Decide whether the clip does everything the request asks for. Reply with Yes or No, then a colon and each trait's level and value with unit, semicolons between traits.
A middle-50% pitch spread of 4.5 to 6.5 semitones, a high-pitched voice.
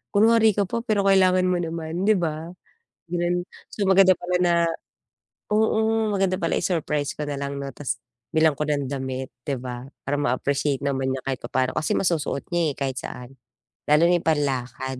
No: average, 5.1 semitones; medium, 155 Hz